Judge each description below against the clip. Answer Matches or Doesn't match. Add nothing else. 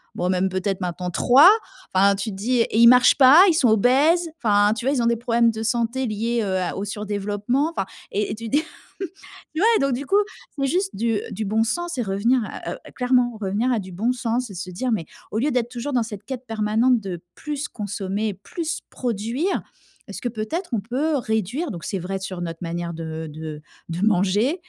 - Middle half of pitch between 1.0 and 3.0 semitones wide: Doesn't match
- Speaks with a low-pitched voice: Doesn't match